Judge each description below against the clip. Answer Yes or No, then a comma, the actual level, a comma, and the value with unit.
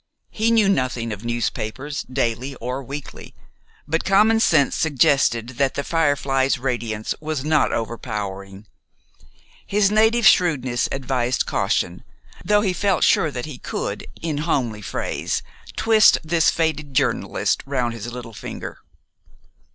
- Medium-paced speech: No, slow, 130 wpm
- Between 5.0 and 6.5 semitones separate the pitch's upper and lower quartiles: Yes, wide, 5.4 semitones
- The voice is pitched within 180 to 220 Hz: No, low, 135 Hz